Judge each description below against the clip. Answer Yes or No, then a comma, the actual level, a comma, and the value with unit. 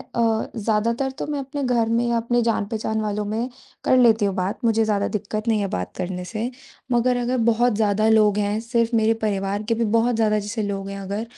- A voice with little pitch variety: Yes, narrow, 2.2 semitones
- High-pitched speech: Yes, high, 220 Hz